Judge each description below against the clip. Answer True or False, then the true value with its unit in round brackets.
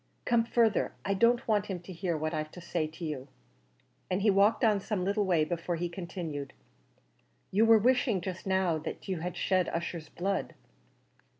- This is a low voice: False (185 Hz)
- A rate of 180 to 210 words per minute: True (185 wpm)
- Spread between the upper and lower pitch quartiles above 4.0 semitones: False (3.4 semitones)